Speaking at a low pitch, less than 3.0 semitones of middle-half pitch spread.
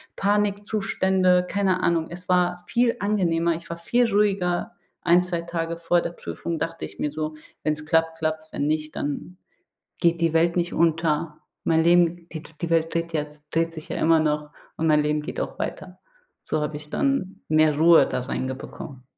No: medium, 165 Hz; narrow, 2.4 semitones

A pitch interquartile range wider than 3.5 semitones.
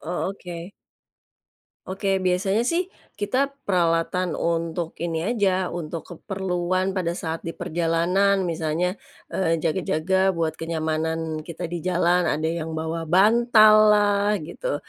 No: average, 2.8 semitones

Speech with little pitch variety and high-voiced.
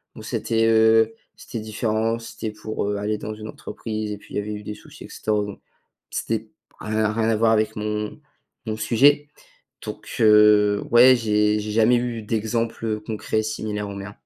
No: narrow, 1.1 semitones; low, 110 Hz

